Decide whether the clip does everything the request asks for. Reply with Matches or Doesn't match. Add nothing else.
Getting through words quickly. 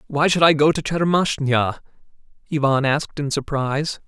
Doesn't match